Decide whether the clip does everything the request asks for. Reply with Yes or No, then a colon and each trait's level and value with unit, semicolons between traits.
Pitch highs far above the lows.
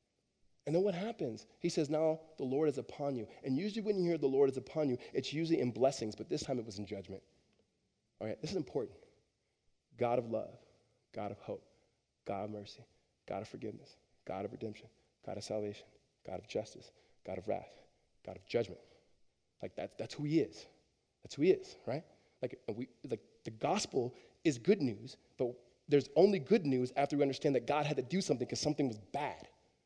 Yes: wide, 5.7 semitones